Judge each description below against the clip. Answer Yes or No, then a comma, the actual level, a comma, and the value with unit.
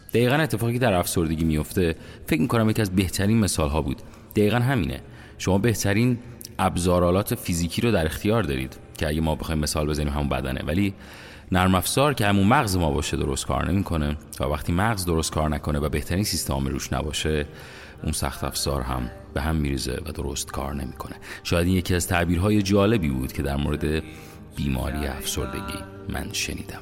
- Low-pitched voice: Yes, very low, 85 Hz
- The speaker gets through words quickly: Yes, fast, 175 wpm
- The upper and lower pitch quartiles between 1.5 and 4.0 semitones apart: No, average, 5.1 semitones